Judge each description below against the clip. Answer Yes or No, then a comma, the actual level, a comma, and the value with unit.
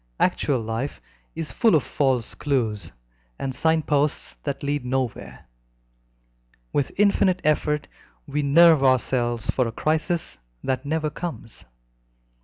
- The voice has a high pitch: No, medium, 140 Hz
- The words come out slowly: Yes, slow, 120 wpm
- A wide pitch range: No, average, 3.9 semitones